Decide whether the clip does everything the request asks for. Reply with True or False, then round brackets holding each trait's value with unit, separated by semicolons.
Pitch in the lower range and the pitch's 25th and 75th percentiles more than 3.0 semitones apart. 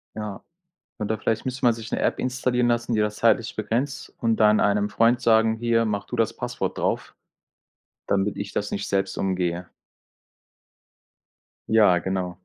False (110 Hz; 2.6 semitones)